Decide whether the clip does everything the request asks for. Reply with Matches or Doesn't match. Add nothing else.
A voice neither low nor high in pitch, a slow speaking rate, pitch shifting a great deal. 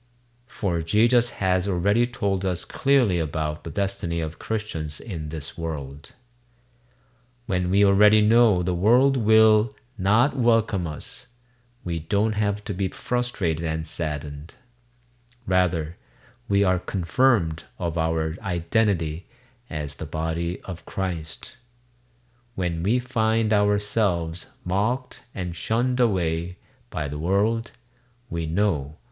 Doesn't match